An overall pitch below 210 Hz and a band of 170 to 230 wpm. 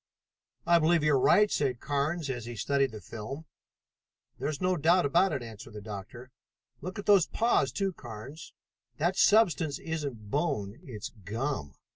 No: medium, 140 Hz; average, 160 wpm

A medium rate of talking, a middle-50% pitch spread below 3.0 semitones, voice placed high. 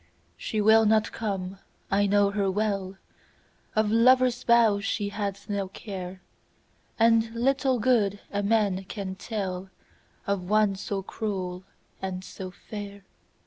No: slow, 115 wpm; narrow, 2.4 semitones; high, 205 Hz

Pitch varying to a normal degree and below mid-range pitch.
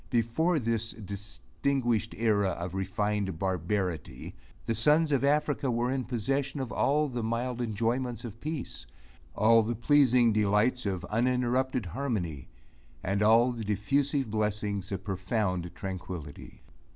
Yes: average, 4.1 semitones; low, 115 Hz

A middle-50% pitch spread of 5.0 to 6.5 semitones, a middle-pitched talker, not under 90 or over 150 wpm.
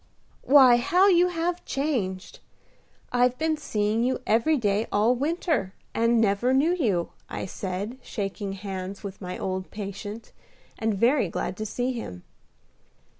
No: wide, 5.4 semitones; high, 225 Hz; average, 140 wpm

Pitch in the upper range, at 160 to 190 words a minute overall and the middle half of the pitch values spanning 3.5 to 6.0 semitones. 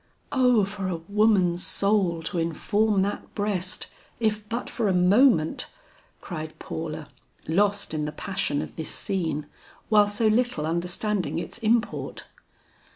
No: high, 195 Hz; slow, 135 wpm; average, 4.3 semitones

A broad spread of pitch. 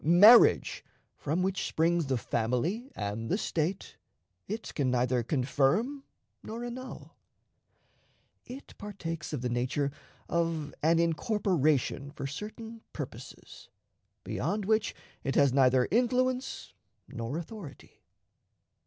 Yes: wide, 8.0 semitones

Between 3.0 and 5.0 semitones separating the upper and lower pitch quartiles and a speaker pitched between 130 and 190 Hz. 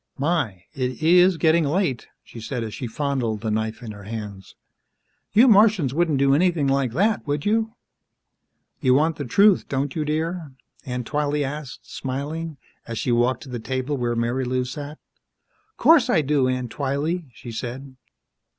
Yes: average, 4.5 semitones; medium, 140 Hz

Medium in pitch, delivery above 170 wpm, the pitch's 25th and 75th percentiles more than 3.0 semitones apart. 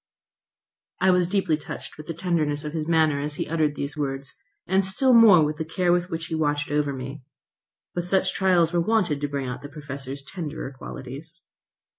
Yes: medium, 155 Hz; average, 195 wpm; average, 3.5 semitones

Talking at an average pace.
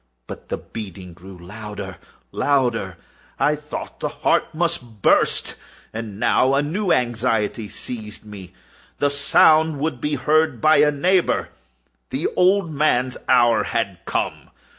No: slow, 130 wpm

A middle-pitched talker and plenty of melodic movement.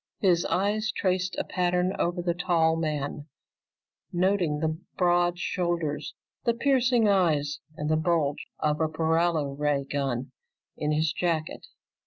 No: medium, 170 Hz; average, 3.1 semitones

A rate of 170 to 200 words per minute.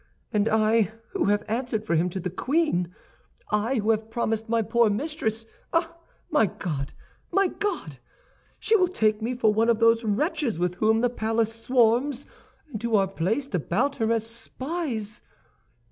No: average, 160 wpm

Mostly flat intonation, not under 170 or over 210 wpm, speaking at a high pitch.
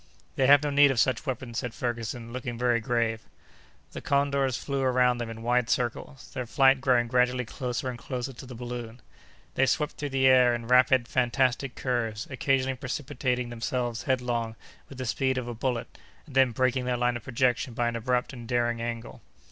No: narrow, 1.7 semitones; average, 190 wpm; low, 125 Hz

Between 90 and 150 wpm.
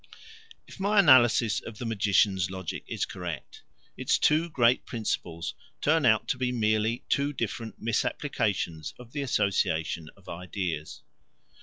Yes: slow, 135 wpm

